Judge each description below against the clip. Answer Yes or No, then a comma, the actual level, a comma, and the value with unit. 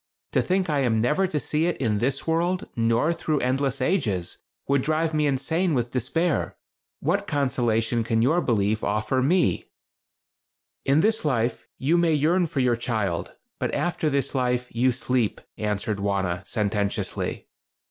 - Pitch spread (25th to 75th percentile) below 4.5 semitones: No, wide, 5.6 semitones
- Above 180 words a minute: No, average, 155 wpm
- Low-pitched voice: Yes, low, 130 Hz